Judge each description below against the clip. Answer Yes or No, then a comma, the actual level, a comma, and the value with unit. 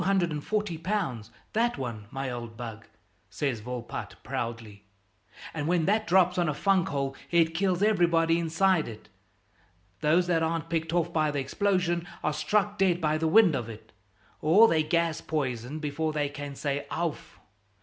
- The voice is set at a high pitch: No, medium, 160 Hz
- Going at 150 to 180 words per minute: Yes, average, 155 wpm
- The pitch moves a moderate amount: Yes, average, 4.3 semitones